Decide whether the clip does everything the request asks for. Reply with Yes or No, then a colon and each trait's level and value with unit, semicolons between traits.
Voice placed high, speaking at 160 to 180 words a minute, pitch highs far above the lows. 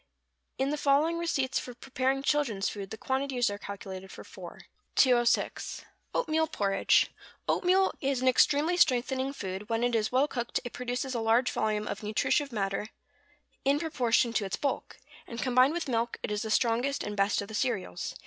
No: high, 245 Hz; average, 175 wpm; average, 4.4 semitones